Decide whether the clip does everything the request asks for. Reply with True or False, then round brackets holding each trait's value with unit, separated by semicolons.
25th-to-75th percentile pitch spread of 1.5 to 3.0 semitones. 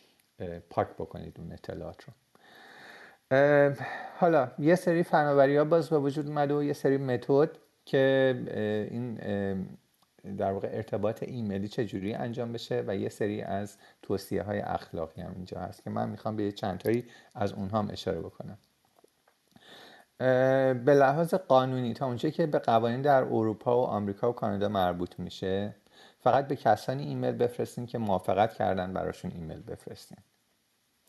False (5.3 semitones)